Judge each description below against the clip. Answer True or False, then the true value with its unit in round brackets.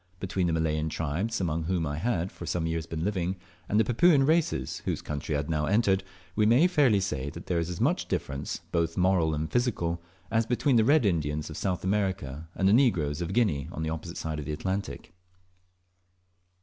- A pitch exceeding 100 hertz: False (90 Hz)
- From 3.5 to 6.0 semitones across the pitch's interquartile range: True (5.0 semitones)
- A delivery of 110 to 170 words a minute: False (205 wpm)